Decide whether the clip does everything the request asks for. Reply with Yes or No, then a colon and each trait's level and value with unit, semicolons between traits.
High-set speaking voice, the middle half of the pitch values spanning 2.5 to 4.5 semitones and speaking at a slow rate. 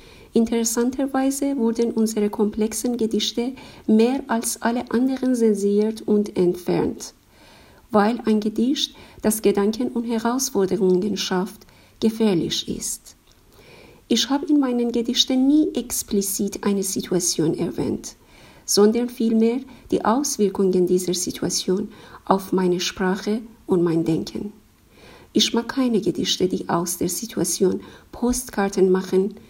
Yes: high, 215 Hz; average, 3.7 semitones; slow, 110 wpm